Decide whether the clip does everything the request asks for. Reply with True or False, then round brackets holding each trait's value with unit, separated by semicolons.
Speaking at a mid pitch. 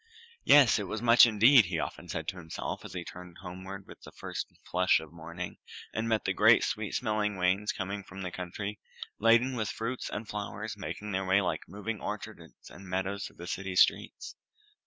False (100 Hz)